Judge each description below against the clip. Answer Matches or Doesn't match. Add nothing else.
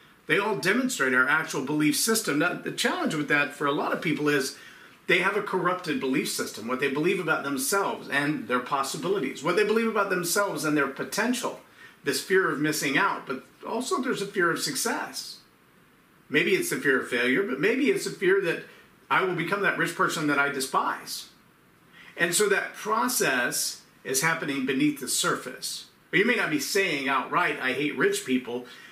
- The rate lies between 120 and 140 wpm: Doesn't match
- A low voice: Doesn't match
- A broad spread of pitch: Matches